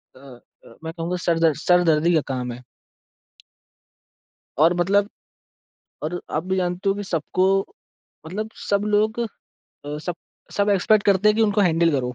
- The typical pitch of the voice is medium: Yes, medium, 175 Hz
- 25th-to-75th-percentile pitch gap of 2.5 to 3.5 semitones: No, average, 4.2 semitones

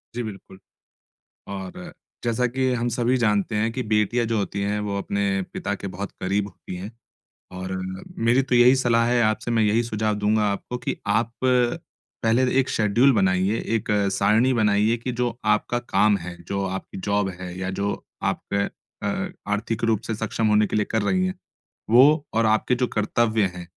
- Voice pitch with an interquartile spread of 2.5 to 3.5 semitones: Yes, average, 2.9 semitones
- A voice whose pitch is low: Yes, low, 110 Hz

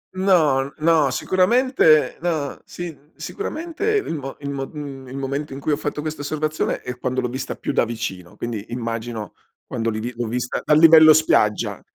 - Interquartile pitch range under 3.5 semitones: No, average, 4.2 semitones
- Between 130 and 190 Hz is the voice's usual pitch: Yes, medium, 140 Hz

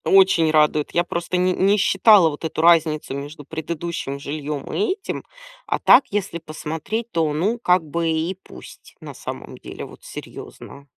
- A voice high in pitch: No, medium, 165 Hz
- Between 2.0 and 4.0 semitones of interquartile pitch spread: Yes, average, 3.7 semitones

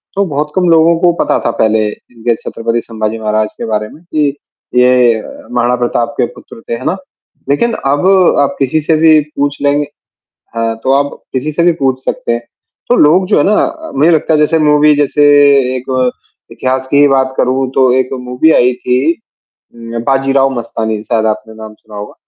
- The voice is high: No, low, 135 Hz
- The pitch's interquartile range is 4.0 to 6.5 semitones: Yes, average, 4.5 semitones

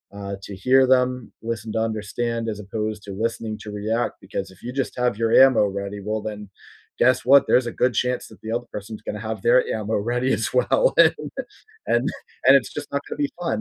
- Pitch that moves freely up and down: No, average, 2.9 semitones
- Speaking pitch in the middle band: No, low, 110 Hz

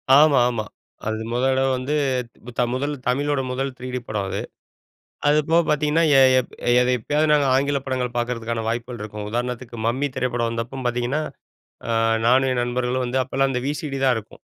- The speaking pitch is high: No, low, 125 Hz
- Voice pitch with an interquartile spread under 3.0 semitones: Yes, narrow, 2.5 semitones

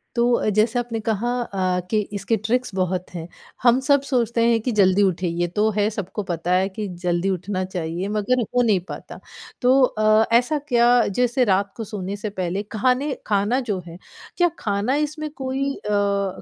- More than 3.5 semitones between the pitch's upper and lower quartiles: Yes, average, 4.2 semitones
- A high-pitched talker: Yes, high, 210 Hz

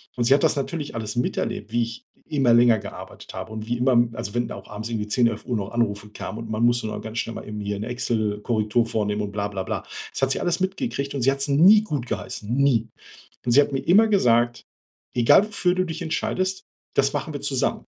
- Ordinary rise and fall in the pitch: Yes, average, 4.4 semitones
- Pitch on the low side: Yes, low, 120 Hz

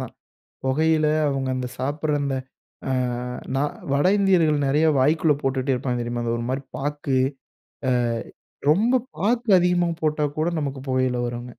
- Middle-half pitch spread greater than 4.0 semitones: No, average, 3.5 semitones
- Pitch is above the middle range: No, medium, 145 Hz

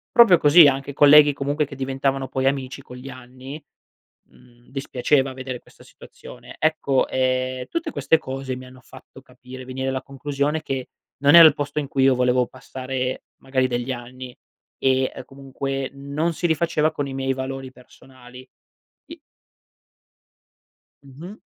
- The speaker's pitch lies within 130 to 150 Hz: Yes, low, 135 Hz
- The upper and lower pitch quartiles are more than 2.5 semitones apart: No, narrow, 1.9 semitones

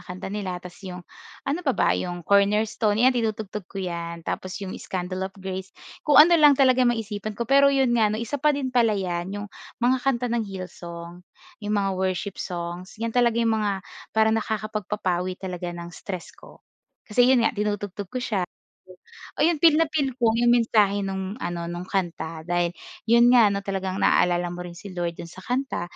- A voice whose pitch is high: Yes, high, 200 Hz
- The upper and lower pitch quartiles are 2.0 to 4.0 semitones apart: No, average, 4.6 semitones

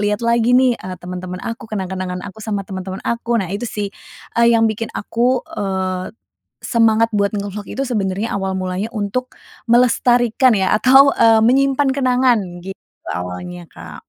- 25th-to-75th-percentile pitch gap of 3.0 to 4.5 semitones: Yes, average, 4.0 semitones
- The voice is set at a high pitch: Yes, high, 215 Hz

